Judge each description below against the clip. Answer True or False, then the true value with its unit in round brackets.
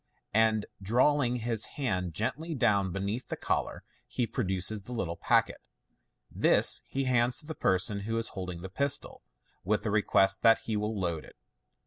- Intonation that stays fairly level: False (4.1 semitones)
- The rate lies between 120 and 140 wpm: False (165 wpm)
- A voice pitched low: True (110 Hz)